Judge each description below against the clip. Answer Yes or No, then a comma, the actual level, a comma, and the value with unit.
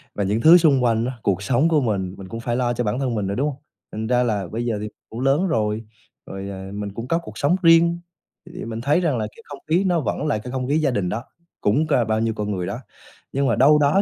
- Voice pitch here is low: Yes, low, 120 Hz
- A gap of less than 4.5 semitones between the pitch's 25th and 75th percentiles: No, wide, 5.4 semitones